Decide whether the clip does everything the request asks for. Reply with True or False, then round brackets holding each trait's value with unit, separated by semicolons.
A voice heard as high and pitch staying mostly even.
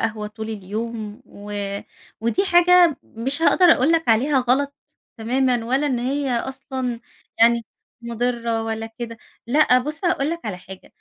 False (245 Hz; 3.9 semitones)